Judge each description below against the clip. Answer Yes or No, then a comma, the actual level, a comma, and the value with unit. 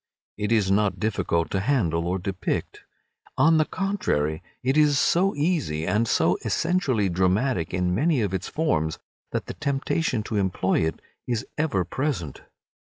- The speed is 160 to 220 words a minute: No, average, 150 wpm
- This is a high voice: No, low, 105 Hz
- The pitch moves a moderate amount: No, wide, 8.1 semitones